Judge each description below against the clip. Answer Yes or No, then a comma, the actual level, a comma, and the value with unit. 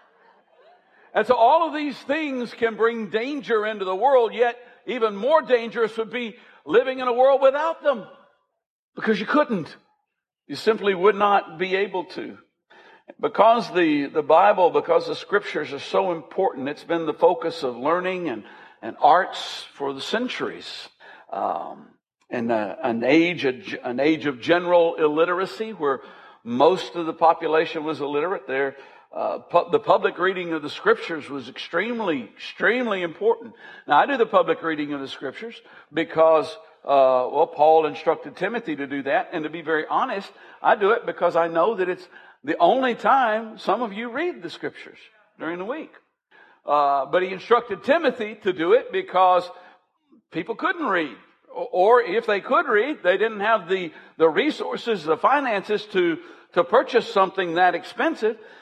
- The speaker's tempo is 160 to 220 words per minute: Yes, average, 165 wpm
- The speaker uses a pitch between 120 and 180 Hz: No, high, 210 Hz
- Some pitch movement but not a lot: No, wide, 7.3 semitones